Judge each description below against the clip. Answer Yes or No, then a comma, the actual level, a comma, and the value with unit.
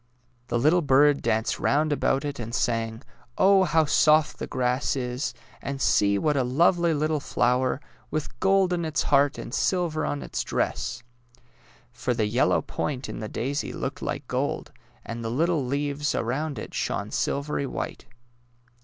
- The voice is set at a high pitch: No, medium, 140 Hz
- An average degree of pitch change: Yes, average, 4.0 semitones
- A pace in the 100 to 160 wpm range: No, average, 170 wpm